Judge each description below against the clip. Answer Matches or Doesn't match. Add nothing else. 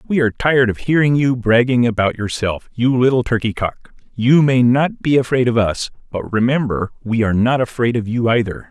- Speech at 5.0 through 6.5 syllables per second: Matches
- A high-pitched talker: Doesn't match